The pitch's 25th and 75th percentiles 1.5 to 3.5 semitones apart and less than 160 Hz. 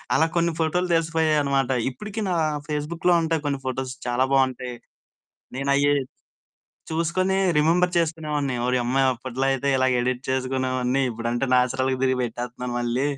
No: average, 4.0 semitones; low, 135 Hz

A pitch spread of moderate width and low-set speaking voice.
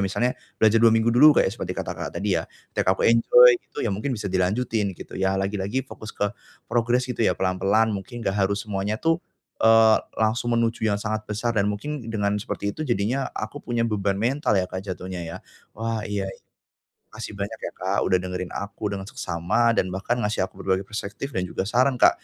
Yes: average, 3.3 semitones; low, 105 Hz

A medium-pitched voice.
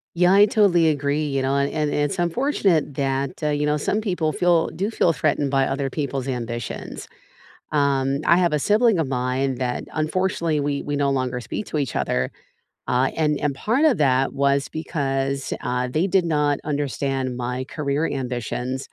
Yes: medium, 145 Hz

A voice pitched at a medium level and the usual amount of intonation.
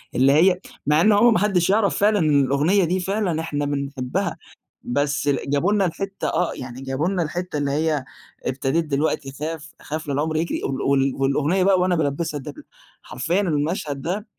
Yes: medium, 155 Hz; average, 4.5 semitones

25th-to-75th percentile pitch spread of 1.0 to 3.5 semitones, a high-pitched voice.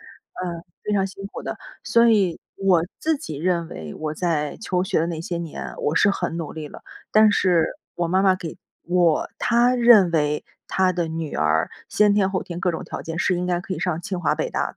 No: average, 3.2 semitones; medium, 180 Hz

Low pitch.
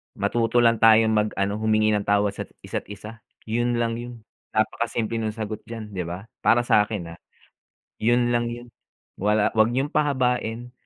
Yes: low, 115 Hz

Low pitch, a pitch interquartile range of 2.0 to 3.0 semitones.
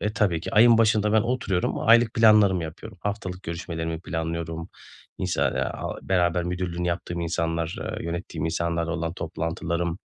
No: very low, 85 Hz; average, 3.6 semitones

